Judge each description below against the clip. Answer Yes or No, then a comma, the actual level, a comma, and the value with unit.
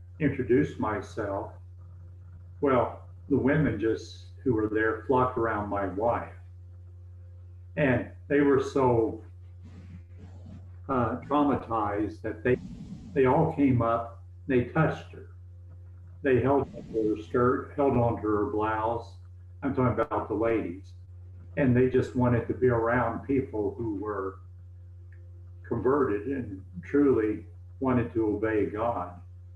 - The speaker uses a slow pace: Yes, slow, 120 wpm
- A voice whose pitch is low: Yes, low, 100 Hz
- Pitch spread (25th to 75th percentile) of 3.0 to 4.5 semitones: No, average, 5.0 semitones